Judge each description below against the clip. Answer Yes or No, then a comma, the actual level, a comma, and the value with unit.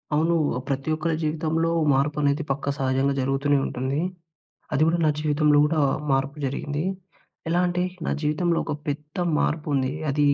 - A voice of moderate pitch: Yes, medium, 150 Hz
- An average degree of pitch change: No, narrow, 2.3 semitones